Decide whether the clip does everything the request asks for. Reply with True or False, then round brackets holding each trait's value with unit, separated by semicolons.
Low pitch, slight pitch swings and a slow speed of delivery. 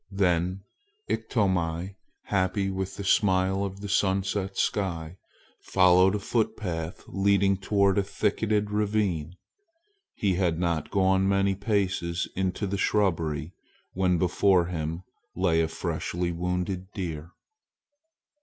True (95 Hz; 2.1 semitones; 115 wpm)